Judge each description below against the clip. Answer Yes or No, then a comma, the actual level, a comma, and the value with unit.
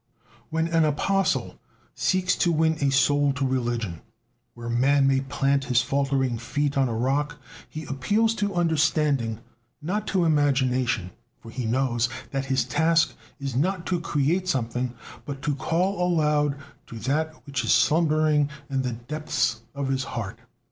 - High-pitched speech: No, medium, 140 Hz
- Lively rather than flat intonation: No, average, 3.7 semitones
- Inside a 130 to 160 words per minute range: Yes, average, 155 wpm